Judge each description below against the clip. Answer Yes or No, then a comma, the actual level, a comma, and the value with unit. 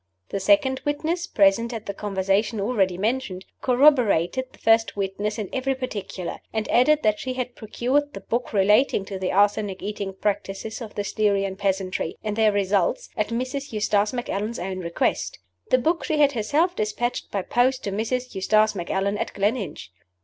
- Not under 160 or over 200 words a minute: Yes, average, 170 wpm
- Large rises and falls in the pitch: No, average, 4.3 semitones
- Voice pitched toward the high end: Yes, high, 215 Hz